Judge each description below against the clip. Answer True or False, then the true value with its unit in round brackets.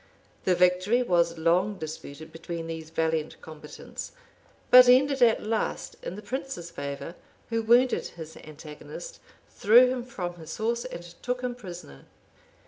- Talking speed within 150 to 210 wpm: False (140 wpm)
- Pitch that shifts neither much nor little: False (7.1 semitones)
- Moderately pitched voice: True (180 Hz)